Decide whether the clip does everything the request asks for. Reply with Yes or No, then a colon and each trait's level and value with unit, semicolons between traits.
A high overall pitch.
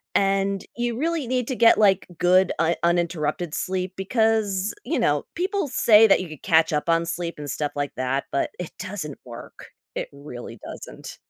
No: medium, 180 Hz